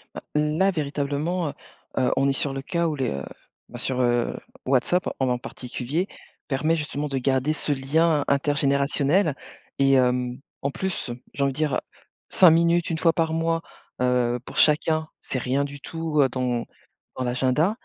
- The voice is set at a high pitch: No, medium, 140 Hz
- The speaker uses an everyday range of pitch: Yes, average, 3.6 semitones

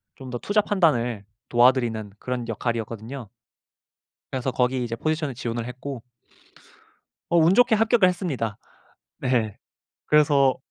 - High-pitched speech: No, low, 130 Hz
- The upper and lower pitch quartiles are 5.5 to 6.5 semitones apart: No, average, 5.1 semitones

